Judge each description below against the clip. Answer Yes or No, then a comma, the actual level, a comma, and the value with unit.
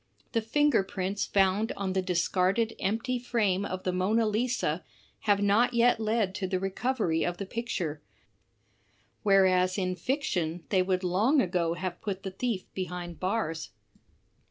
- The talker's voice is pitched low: No, high, 195 Hz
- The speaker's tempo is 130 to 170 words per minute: Yes, average, 150 wpm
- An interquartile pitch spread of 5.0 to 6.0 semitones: No, average, 3.5 semitones